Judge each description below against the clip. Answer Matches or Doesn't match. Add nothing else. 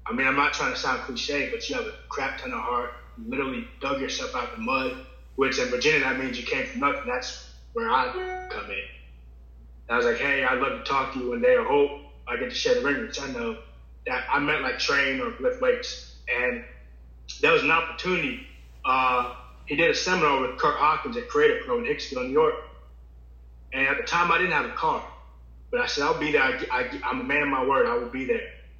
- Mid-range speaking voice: Matches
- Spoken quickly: Matches